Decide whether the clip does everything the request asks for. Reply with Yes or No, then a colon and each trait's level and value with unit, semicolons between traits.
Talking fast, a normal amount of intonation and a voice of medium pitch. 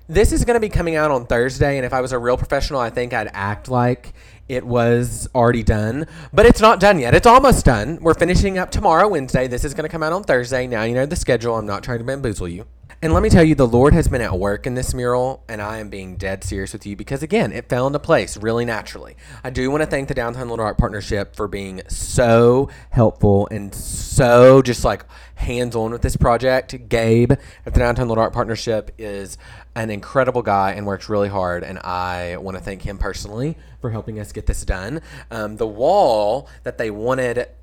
No: fast, 230 wpm; average, 4.2 semitones; low, 120 Hz